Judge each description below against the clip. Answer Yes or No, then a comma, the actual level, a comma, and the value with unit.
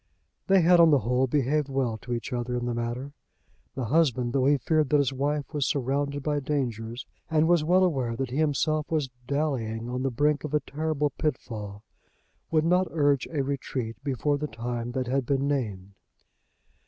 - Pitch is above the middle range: No, medium, 140 Hz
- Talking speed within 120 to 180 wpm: No, average, 190 wpm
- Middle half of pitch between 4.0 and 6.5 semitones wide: No, average, 3.6 semitones